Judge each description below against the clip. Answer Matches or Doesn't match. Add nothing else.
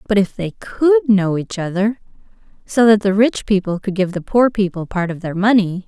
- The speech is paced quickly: Matches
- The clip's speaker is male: Doesn't match